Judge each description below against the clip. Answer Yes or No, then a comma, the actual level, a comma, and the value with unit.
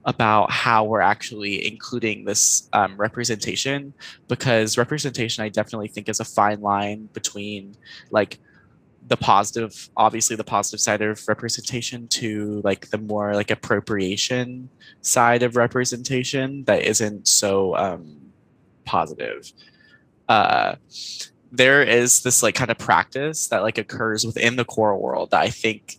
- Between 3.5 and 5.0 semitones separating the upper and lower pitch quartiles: No, narrow, 2.6 semitones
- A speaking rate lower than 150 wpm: Yes, slow, 135 wpm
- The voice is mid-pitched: No, low, 110 Hz